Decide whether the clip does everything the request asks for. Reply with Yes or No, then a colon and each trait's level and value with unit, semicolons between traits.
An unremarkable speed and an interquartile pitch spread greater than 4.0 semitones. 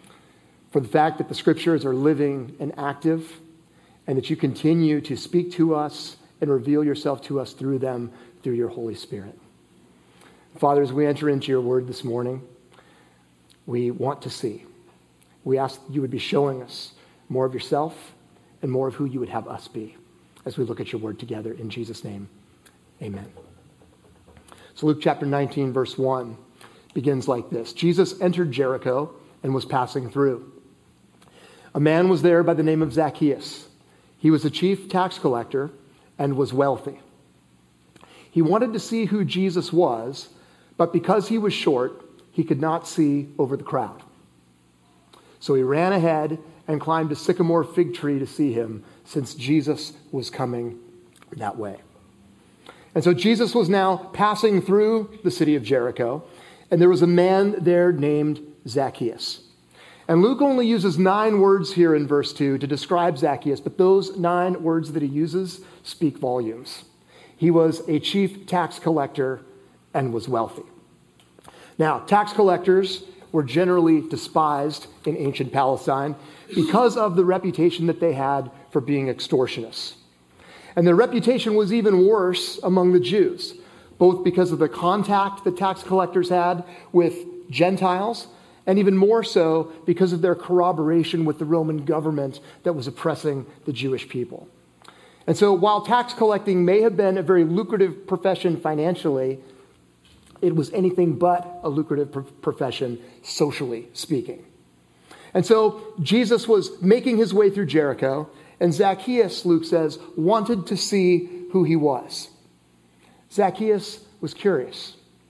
Yes: average, 155 wpm; average, 5.3 semitones